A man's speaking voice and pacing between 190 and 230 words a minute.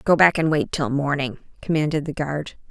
No: female; average, 200 wpm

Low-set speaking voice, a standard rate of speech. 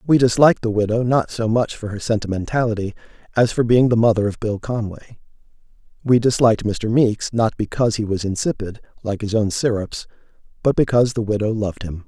Yes: low, 110 Hz; average, 185 wpm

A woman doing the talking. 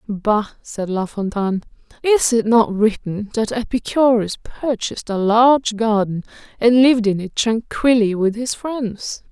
Yes: female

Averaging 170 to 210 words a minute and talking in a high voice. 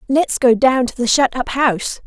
No: fast, 235 wpm; very high, 255 Hz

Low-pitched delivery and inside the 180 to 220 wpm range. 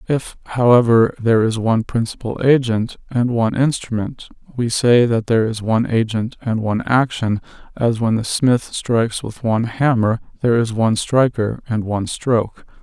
No: low, 115 Hz; average, 165 wpm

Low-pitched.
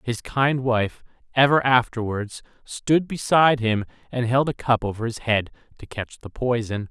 Yes: low, 120 Hz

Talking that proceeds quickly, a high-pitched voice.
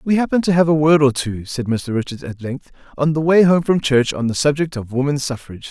No: fast, 265 wpm; medium, 140 Hz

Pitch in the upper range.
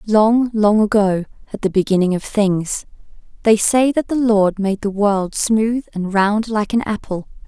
Yes: high, 210 Hz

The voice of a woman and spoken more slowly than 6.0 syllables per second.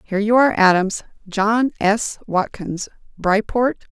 Yes: female; 4.4 syllables/s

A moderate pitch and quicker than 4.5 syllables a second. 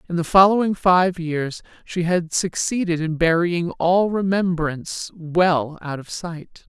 No: medium, 170 Hz; 3.9 syllables/s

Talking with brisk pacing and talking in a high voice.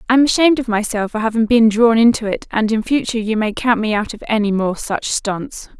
Yes: fast, 240 wpm; high, 225 Hz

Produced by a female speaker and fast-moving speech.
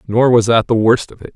No: male; fast, 310 wpm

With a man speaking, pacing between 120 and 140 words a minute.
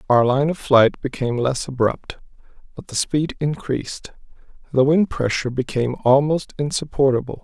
Yes: male; slow, 135 wpm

